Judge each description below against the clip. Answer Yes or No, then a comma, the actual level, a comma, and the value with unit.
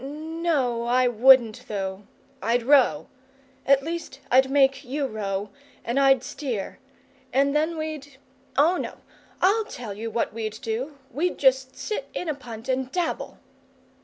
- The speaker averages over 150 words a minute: No, average, 145 wpm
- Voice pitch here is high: Yes, very high, 265 Hz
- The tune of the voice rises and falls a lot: No, average, 4.2 semitones